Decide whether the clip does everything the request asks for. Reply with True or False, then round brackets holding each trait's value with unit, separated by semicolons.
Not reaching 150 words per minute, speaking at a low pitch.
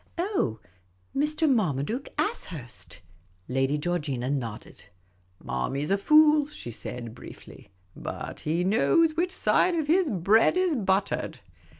False (135 wpm; 195 Hz)